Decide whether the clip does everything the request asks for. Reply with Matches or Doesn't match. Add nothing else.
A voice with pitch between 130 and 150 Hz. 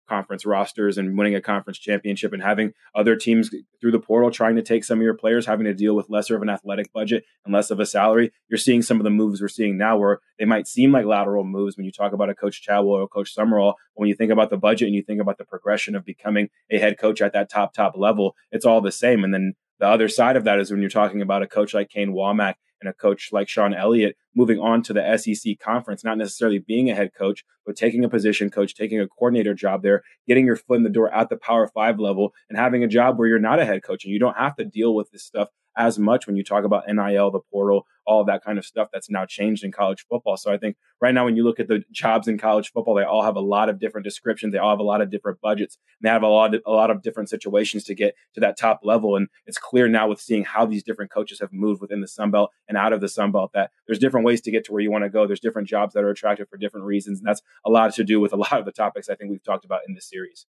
Doesn't match